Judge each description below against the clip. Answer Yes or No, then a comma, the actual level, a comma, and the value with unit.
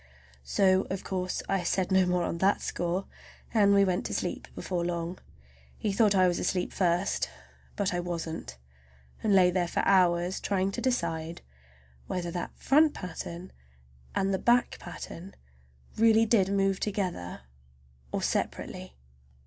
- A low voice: No, medium, 185 Hz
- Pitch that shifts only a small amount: Yes, narrow, 2.3 semitones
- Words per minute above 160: No, average, 145 wpm